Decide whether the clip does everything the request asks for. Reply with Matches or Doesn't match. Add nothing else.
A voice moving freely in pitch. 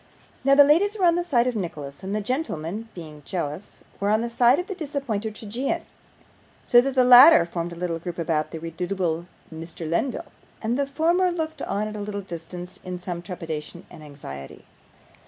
Matches